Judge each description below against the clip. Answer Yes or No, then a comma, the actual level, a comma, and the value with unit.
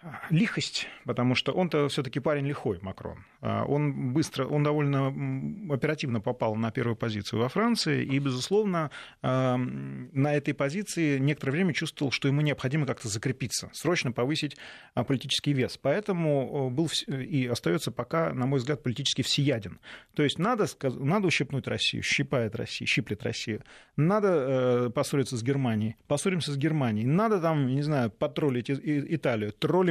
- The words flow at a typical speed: Yes, average, 140 wpm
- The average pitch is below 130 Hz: No, medium, 140 Hz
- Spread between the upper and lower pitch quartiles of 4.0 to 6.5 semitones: No, average, 3.6 semitones